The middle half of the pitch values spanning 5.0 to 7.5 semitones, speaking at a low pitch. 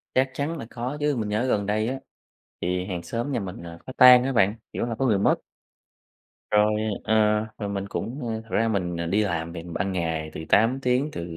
Yes: wide, 5.5 semitones; low, 105 Hz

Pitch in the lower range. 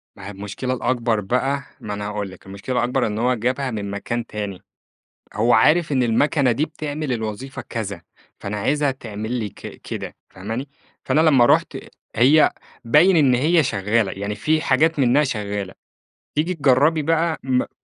Yes: low, 125 Hz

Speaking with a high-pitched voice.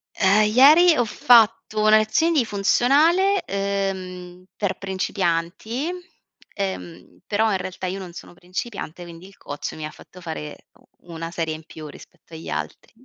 Yes: high, 195 Hz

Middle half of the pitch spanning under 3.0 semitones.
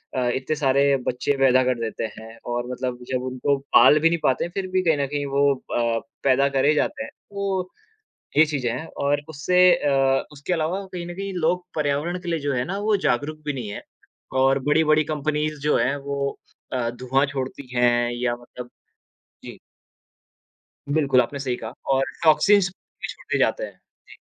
No: average, 3.7 semitones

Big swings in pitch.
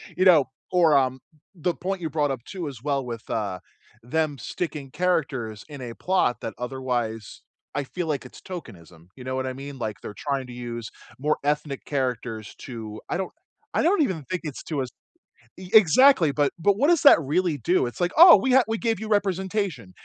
Yes: wide, 6.7 semitones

